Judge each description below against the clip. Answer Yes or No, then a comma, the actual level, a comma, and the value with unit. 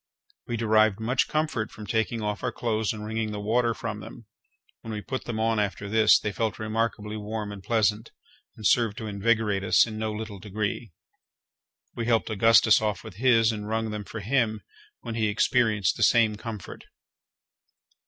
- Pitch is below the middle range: Yes, low, 110 Hz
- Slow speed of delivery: No, average, 180 wpm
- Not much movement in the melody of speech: Yes, narrow, 1.4 semitones